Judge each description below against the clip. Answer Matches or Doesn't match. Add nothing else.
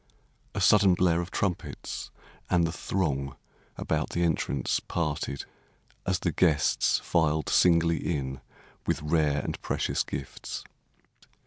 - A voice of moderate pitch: Doesn't match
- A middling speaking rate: Doesn't match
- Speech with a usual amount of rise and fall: Matches